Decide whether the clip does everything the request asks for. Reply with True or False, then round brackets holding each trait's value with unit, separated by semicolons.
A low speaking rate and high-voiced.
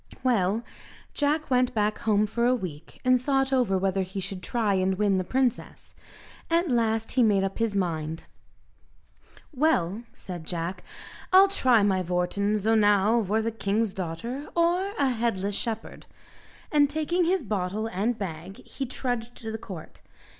False (160 wpm; 220 Hz)